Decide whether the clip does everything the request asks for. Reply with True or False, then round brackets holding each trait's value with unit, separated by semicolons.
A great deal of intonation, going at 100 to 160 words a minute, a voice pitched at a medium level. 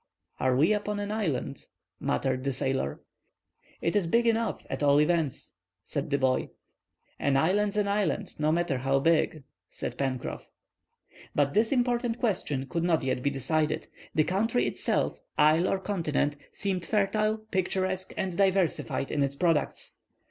True (6.3 semitones; 150 wpm; 170 Hz)